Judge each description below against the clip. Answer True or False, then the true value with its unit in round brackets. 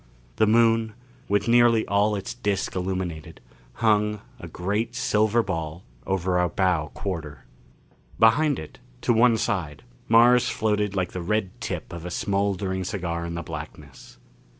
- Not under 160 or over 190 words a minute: False (145 wpm)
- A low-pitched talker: True (100 Hz)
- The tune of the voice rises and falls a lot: False (4.0 semitones)